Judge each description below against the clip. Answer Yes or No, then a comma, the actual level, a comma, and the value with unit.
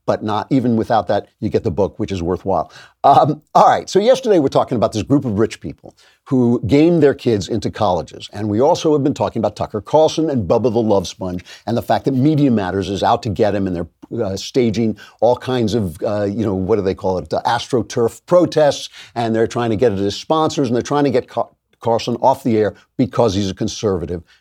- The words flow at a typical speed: No, fast, 235 wpm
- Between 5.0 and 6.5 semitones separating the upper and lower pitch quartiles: No, average, 4.4 semitones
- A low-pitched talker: Yes, low, 115 Hz